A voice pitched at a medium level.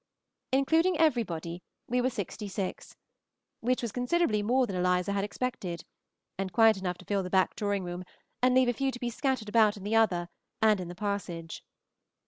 No: high, 210 Hz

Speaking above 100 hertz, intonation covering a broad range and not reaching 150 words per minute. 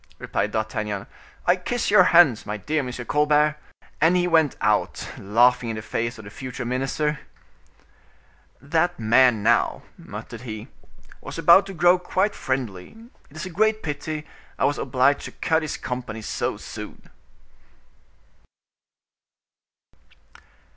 Yes: medium, 140 Hz; wide, 6.2 semitones; slow, 135 wpm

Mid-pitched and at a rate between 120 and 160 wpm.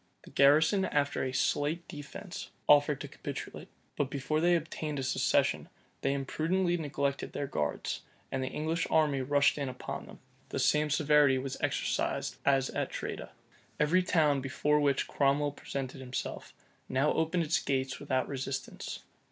Yes: medium, 145 Hz; average, 150 wpm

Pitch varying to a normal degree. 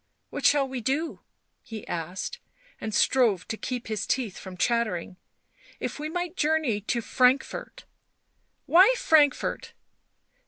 No: wide, 5.9 semitones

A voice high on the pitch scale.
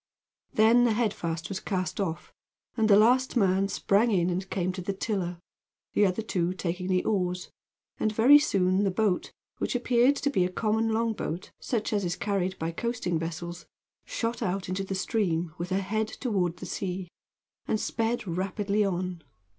Yes: high, 195 Hz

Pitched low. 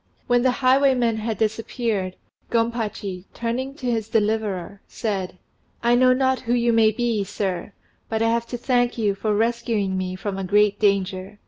No: high, 220 Hz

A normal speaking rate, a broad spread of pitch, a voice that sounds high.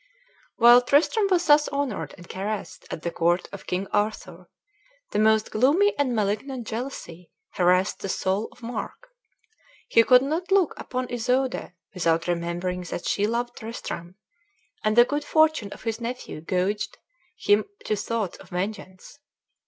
Yes: average, 150 wpm; wide, 5.8 semitones; high, 220 Hz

